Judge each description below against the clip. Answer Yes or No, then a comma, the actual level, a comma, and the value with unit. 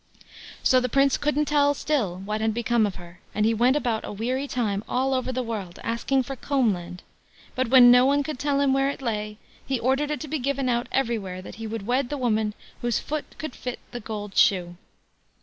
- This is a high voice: Yes, high, 245 Hz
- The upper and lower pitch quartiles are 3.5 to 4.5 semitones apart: Yes, average, 4.1 semitones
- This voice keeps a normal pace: No, fast, 220 wpm